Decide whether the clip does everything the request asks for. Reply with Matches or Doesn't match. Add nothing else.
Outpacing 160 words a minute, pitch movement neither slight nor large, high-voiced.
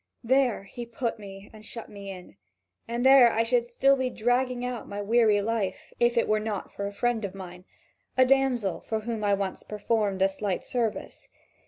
Matches